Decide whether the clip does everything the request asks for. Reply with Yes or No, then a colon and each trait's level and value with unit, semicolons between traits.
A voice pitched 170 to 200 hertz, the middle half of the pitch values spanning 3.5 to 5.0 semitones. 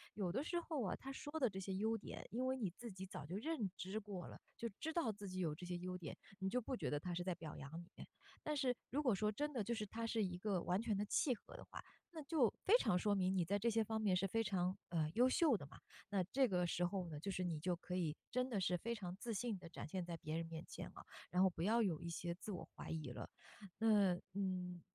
Yes: high, 195 Hz; average, 4.5 semitones